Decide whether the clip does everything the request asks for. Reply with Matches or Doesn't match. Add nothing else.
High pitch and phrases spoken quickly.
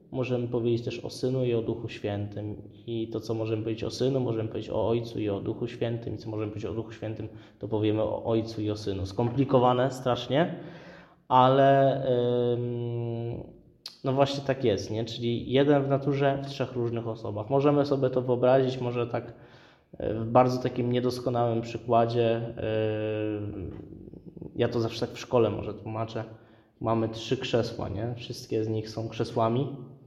Doesn't match